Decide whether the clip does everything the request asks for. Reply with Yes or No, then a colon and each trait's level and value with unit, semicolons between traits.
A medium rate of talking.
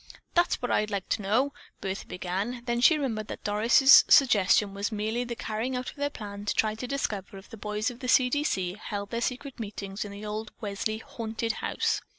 No: fast, 215 wpm